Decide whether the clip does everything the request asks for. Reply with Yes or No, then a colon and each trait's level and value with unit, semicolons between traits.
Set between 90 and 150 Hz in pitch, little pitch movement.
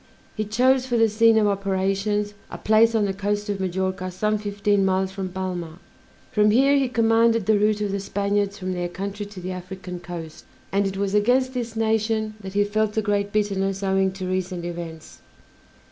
No: high, 200 Hz; narrow, 2.2 semitones